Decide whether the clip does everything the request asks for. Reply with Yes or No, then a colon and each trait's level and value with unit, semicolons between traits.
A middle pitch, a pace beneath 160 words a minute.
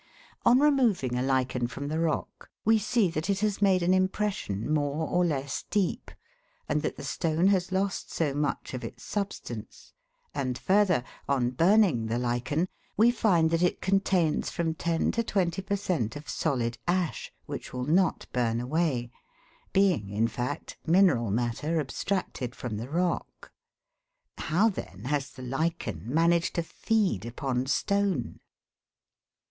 Yes: medium, 160 Hz; average, 150 wpm